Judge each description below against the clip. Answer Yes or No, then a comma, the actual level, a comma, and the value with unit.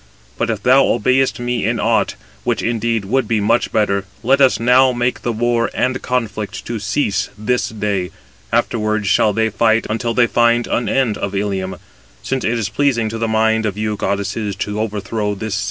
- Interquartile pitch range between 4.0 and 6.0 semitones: No, narrow, 2.6 semitones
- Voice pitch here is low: Yes, low, 110 Hz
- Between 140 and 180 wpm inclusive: No, average, 190 wpm